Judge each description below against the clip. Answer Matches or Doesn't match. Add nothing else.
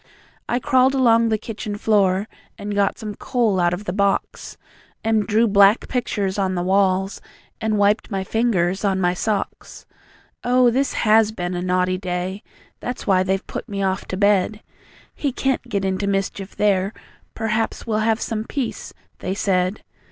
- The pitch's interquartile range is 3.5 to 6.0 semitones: Doesn't match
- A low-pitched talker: Doesn't match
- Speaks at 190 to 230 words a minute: Doesn't match